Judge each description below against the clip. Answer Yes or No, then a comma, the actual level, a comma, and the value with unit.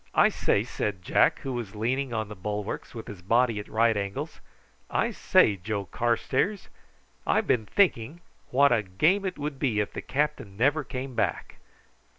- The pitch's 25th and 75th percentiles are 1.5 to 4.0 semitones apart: No, average, 4.7 semitones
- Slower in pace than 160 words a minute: No, average, 170 wpm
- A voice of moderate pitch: No, low, 115 Hz